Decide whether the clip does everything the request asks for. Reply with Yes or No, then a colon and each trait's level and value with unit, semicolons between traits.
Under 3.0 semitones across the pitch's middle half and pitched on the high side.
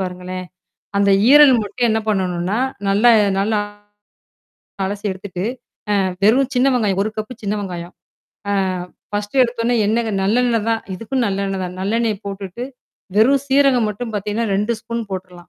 No: average, 3.4 semitones; high, 210 Hz